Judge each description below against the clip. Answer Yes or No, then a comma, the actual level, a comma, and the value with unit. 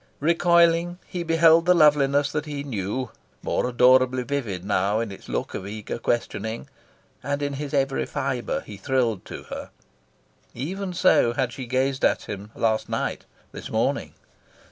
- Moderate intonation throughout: Yes, average, 4.5 semitones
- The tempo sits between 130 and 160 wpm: Yes, average, 155 wpm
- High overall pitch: No, low, 135 Hz